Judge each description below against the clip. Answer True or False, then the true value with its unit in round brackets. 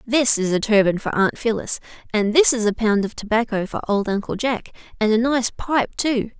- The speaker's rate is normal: False (215 wpm)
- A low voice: False (225 Hz)